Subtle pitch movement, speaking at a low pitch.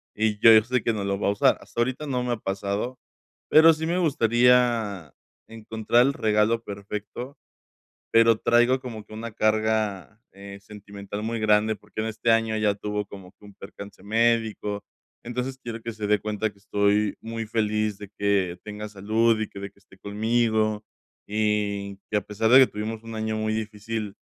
Yes: narrow, 1.9 semitones; low, 110 Hz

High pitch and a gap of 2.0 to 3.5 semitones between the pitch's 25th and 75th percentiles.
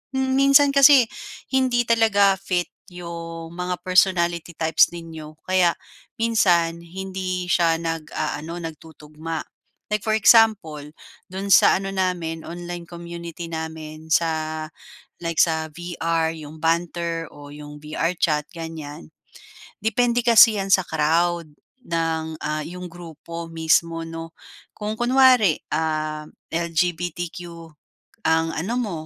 No: medium, 170 Hz; average, 2.7 semitones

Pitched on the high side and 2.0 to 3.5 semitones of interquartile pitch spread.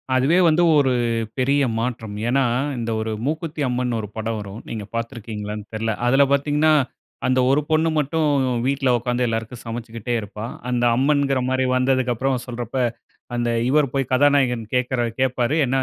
No: low, 125 Hz; average, 3.1 semitones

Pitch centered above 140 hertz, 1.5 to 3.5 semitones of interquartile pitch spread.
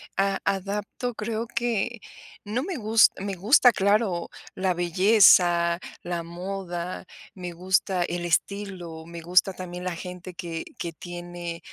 Yes: medium, 185 Hz; average, 2.8 semitones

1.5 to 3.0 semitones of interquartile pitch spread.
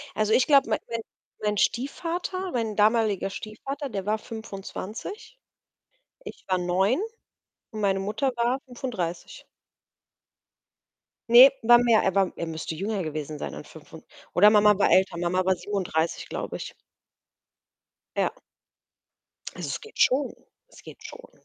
No: average, 4.7 semitones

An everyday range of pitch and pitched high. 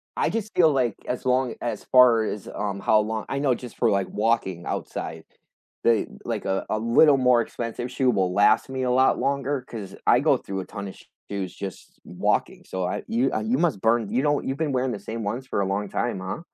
No: average, 4.2 semitones; low, 115 Hz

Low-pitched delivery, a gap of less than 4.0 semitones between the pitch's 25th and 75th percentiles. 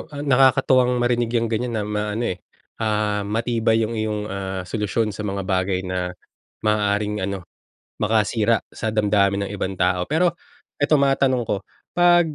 Yes: low, 105 Hz; average, 3.5 semitones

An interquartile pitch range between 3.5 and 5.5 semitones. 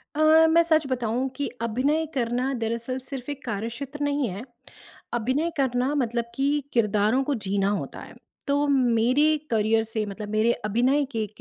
Yes: average, 4.2 semitones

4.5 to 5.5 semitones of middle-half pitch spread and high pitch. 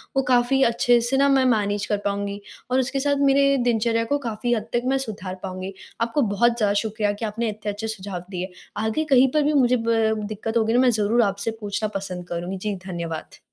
No: average, 3.1 semitones; high, 220 Hz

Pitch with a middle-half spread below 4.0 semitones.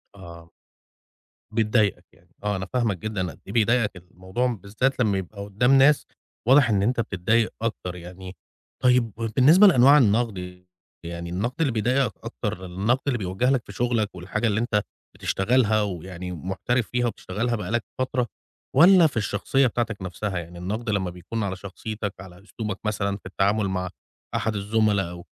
No: average, 4.3 semitones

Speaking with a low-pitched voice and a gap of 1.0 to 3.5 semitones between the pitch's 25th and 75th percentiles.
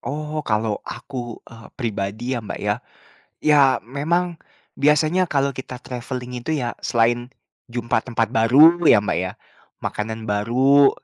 No: low, 125 Hz; average, 4.1 semitones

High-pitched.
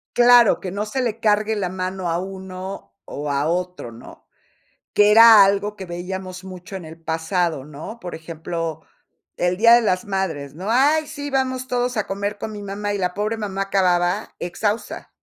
Yes: high, 195 Hz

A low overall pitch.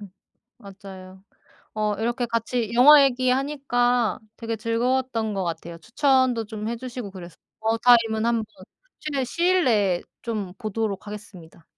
No: high, 230 Hz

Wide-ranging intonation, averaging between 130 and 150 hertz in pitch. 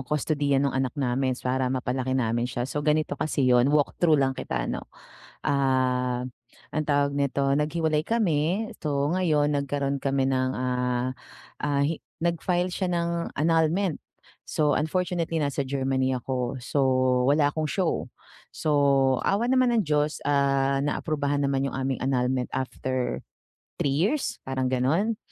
No: average, 3.1 semitones; medium, 140 Hz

